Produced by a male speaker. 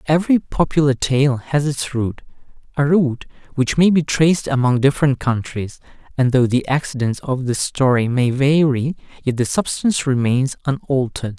Yes: male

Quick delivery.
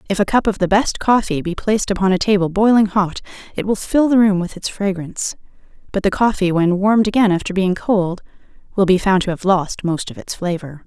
Yes: fast, 225 wpm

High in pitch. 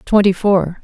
Yes: high, 195 Hz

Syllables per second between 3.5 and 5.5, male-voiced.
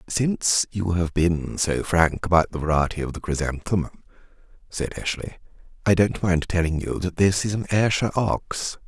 Yes: 5.0 syllables/s; male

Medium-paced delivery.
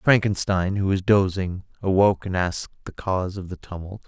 Yes: average, 175 wpm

